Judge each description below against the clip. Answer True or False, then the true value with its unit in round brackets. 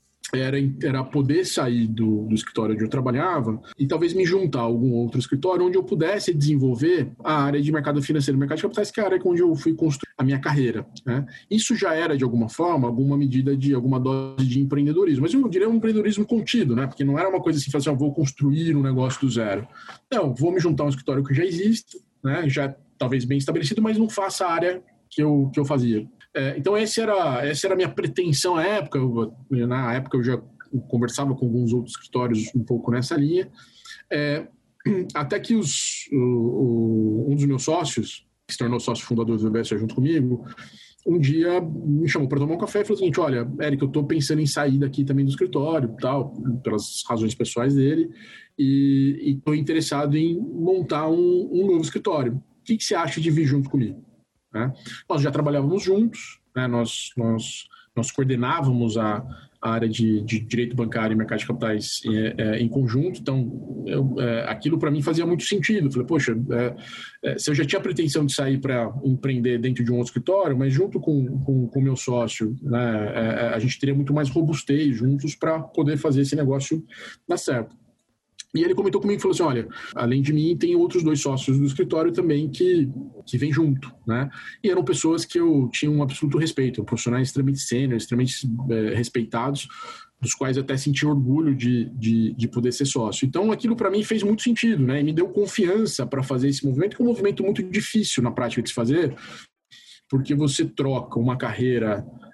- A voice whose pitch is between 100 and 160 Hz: True (140 Hz)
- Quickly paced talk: True (205 wpm)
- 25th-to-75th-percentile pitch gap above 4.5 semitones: True (5.1 semitones)